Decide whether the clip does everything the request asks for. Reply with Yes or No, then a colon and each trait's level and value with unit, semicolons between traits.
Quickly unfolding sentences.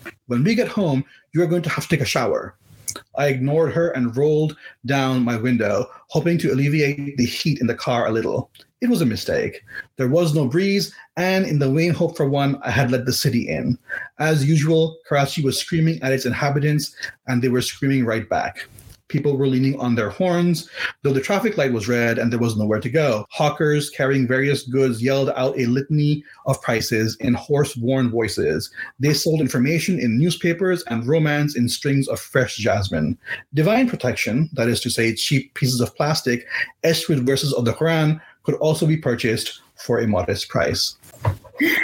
No: average, 190 wpm